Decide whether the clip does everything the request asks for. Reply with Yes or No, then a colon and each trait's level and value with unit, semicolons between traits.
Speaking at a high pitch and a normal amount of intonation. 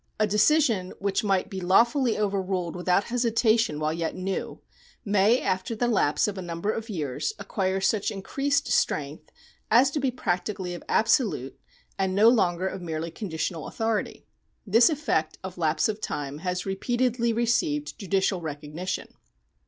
Yes: high, 195 Hz; average, 4.5 semitones